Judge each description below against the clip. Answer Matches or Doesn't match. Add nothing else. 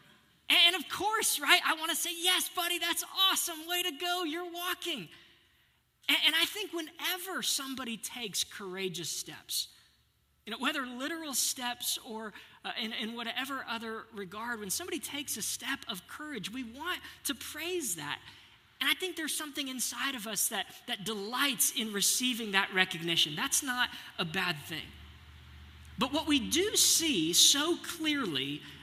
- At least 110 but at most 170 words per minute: Matches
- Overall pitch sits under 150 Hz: Doesn't match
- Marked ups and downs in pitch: Matches